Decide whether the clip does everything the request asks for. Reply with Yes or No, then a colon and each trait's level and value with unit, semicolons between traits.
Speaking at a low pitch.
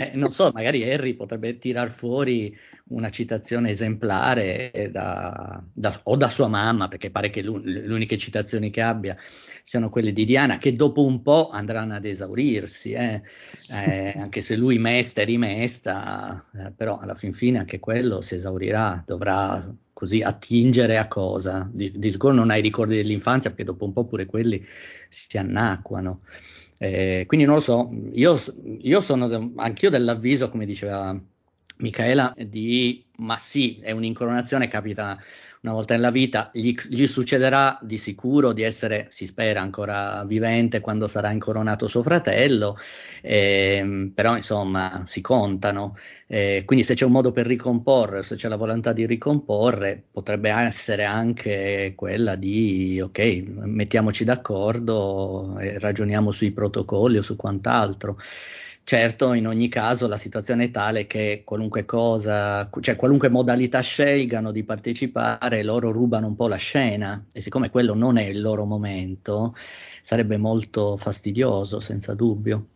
Yes: low, 110 Hz